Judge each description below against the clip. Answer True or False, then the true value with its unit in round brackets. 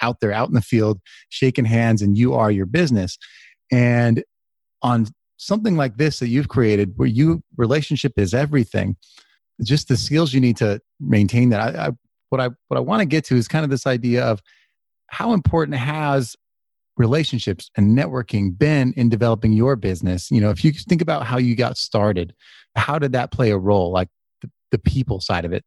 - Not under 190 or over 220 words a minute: True (195 wpm)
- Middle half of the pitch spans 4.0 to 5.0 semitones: True (4.4 semitones)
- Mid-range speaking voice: False (120 Hz)